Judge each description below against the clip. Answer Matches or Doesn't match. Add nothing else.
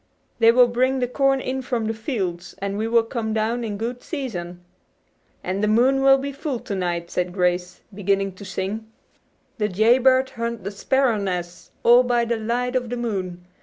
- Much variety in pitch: Doesn't match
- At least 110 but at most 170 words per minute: Doesn't match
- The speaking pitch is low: Doesn't match